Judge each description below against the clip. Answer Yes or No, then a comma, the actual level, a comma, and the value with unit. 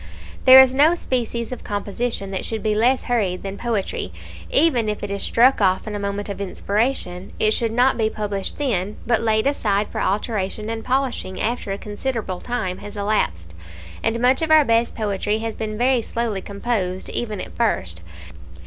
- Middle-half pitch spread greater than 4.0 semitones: No, average, 3.3 semitones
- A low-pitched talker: No, high, 215 Hz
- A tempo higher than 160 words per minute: Yes, average, 185 wpm